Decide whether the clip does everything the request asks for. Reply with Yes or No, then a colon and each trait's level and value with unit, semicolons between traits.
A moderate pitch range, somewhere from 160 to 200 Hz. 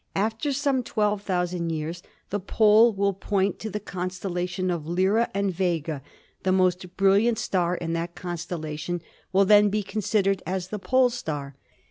Yes: average, 3.0 semitones; high, 190 Hz